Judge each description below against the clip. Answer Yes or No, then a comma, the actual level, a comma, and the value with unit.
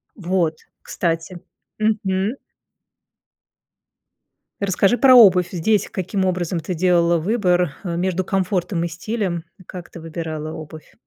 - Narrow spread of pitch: Yes, narrow, 2.3 semitones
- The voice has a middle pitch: Yes, medium, 180 Hz